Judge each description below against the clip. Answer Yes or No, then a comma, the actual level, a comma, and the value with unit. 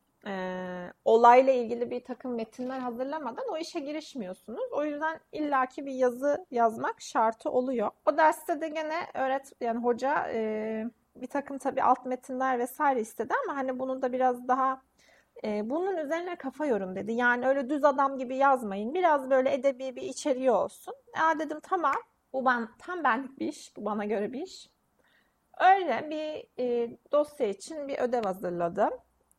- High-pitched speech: Yes, very high, 265 Hz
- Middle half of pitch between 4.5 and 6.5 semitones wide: No, average, 4.0 semitones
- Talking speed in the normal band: No, fast, 160 wpm